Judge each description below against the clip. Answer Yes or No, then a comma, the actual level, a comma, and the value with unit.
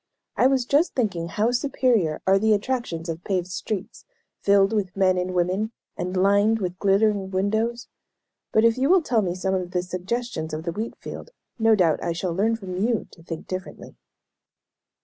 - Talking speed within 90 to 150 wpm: No, average, 185 wpm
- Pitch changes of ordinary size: Yes, average, 3.8 semitones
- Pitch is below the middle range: No, high, 195 Hz